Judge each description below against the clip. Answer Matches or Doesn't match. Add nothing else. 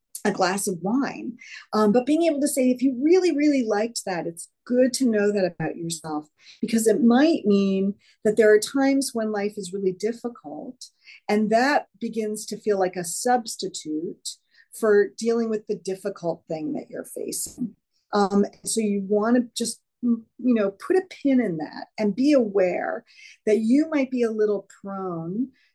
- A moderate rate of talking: Matches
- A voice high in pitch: Matches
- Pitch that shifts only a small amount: Doesn't match